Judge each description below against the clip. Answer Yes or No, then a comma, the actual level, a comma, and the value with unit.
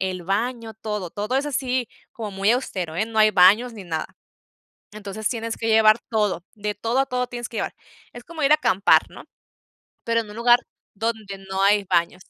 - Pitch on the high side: Yes, high, 220 Hz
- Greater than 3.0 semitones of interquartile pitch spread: Yes, average, 3.4 semitones